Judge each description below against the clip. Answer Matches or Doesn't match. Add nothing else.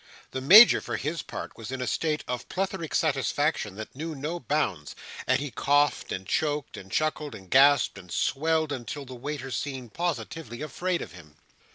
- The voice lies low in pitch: Doesn't match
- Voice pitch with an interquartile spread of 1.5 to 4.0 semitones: Doesn't match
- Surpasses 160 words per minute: Matches